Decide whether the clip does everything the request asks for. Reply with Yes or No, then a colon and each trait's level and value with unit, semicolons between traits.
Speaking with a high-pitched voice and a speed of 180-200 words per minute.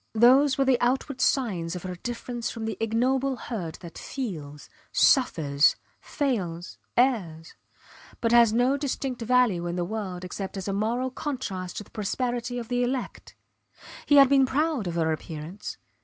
No: high, 230 Hz; average, 160 wpm